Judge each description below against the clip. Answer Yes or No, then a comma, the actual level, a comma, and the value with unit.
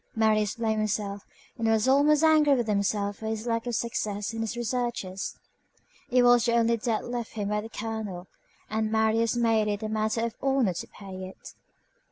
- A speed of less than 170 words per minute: No, average, 190 wpm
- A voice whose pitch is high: Yes, high, 220 Hz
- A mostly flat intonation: Yes, narrow, 2.1 semitones